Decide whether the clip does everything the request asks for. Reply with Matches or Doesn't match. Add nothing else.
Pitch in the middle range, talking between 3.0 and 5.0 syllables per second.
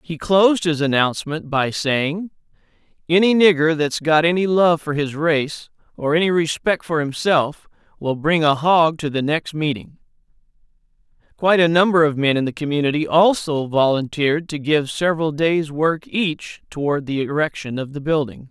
Matches